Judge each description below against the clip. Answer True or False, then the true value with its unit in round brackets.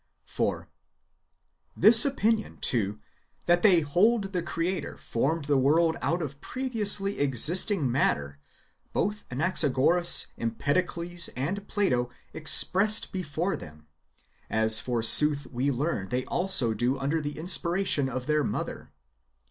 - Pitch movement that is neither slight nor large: False (6.3 semitones)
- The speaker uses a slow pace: True (115 wpm)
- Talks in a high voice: False (155 Hz)